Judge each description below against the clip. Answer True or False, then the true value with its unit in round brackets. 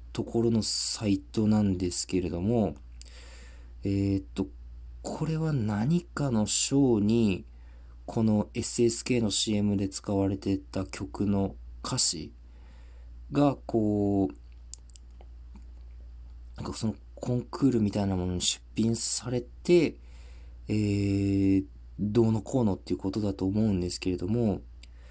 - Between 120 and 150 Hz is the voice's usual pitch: False (95 Hz)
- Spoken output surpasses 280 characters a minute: False (225 characters per minute)